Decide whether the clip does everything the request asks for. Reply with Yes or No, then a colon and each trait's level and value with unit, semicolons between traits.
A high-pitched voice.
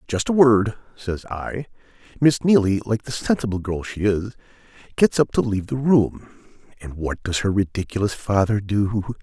No: low, 105 Hz